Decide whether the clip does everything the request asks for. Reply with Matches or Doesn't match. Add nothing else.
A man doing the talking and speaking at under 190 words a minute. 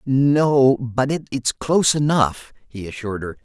Matches